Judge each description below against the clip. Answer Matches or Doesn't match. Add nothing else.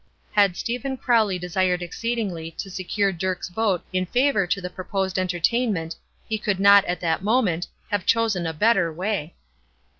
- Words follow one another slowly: Doesn't match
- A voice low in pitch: Doesn't match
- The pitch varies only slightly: Doesn't match